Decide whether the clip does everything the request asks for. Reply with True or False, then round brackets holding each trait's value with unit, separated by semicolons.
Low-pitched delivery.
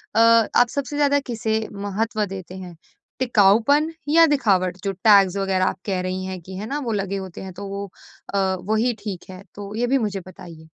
False (200 Hz)